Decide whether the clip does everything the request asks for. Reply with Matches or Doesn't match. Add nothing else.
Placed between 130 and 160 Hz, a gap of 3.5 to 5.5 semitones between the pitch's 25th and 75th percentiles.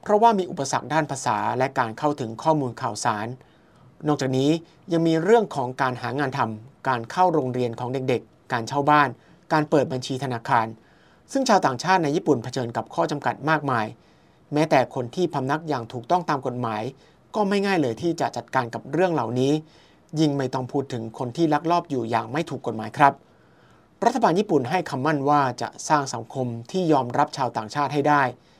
Matches